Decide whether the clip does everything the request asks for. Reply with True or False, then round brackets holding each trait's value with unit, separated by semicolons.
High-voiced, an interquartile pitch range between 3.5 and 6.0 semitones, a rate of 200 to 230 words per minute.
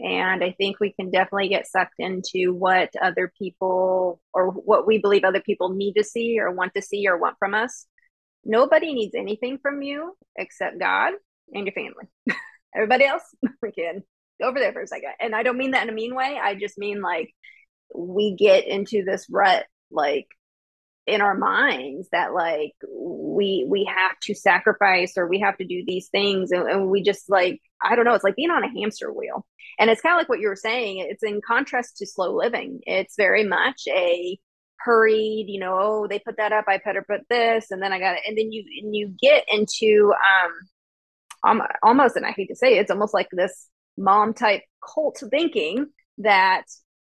True (205 Hz; 4.2 semitones; 205 wpm)